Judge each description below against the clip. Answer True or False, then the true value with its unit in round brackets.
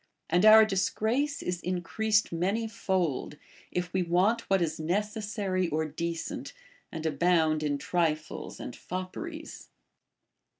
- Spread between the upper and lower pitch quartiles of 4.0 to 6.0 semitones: True (4.4 semitones)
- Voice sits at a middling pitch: True (180 Hz)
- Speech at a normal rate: False (125 wpm)